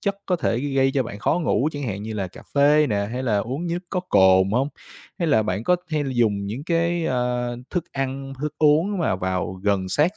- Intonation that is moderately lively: No, wide, 6.9 semitones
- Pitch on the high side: No, low, 135 Hz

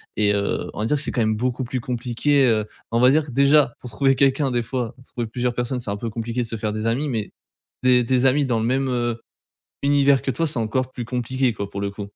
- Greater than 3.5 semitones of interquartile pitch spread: No, average, 2.7 semitones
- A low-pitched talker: Yes, low, 125 Hz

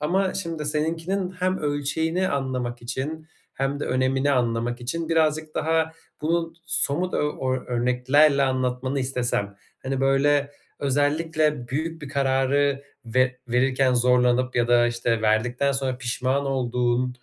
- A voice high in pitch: No, low, 135 Hz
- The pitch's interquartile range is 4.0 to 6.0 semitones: No, average, 3.4 semitones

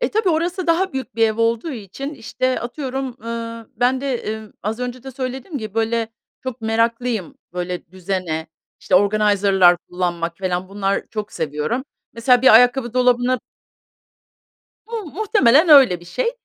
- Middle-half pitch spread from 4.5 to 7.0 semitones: Yes, average, 4.8 semitones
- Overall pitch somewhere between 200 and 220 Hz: No, high, 230 Hz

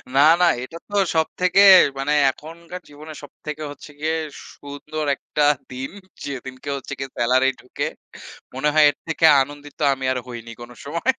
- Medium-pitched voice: Yes, medium, 145 Hz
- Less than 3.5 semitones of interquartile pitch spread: Yes, average, 2.9 semitones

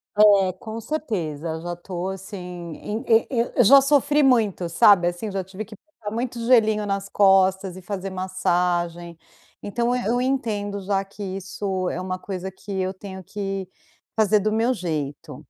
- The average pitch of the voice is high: Yes, high, 195 Hz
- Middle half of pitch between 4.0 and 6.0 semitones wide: No, average, 3.0 semitones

